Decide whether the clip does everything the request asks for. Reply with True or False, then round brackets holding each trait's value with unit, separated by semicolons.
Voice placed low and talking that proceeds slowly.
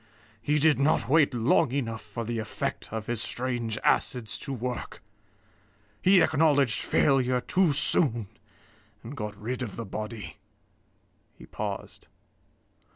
True (125 Hz; 130 wpm)